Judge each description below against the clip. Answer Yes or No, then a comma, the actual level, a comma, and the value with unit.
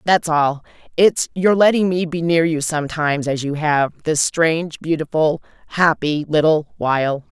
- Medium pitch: Yes, medium, 155 Hz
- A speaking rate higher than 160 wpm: No, average, 155 wpm